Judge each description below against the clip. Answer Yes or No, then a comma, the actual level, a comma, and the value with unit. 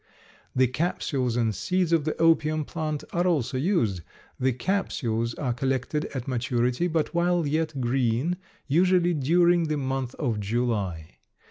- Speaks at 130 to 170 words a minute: Yes, average, 140 wpm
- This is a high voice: No, medium, 140 Hz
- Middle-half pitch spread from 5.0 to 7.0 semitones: Yes, wide, 5.5 semitones